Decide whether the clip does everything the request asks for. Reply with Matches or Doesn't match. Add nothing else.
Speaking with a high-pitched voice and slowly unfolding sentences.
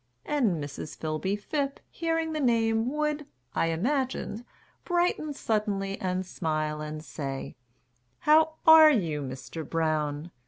Matches